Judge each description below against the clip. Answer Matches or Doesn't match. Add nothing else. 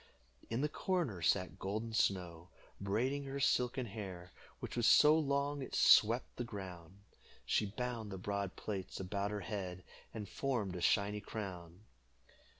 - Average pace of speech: Matches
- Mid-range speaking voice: Doesn't match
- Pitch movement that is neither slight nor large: Matches